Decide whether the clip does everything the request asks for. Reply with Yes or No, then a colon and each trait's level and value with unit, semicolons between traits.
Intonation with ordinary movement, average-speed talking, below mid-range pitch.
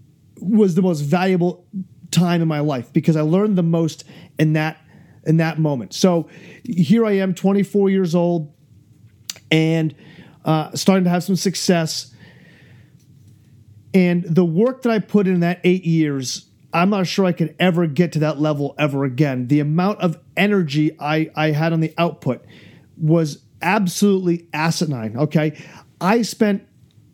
No: average, 3.4 semitones; average, 155 wpm; medium, 165 Hz